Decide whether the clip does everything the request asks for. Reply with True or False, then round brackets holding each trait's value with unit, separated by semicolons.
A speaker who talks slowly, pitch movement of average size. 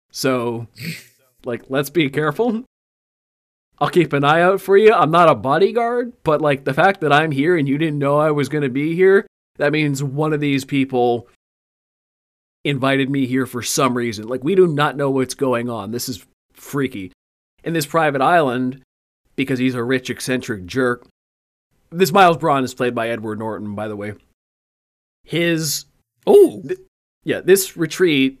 False (175 wpm; 4.7 semitones)